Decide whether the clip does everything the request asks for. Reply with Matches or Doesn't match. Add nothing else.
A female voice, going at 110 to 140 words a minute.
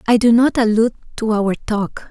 Doesn't match